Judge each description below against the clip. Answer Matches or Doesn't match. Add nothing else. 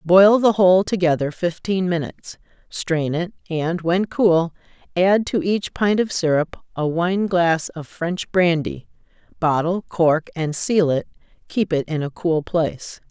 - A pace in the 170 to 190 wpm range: Doesn't match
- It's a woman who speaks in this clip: Matches